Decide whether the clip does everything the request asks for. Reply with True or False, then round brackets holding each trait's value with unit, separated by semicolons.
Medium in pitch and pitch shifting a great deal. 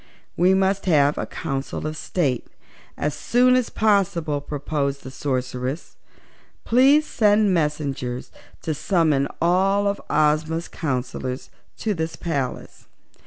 True (155 Hz; 5.7 semitones)